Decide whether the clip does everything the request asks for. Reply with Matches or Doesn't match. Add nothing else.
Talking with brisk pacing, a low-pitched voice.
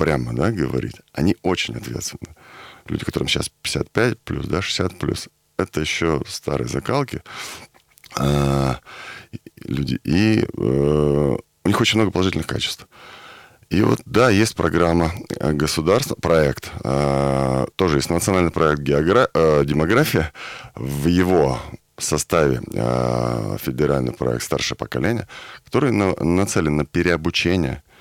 Doesn't match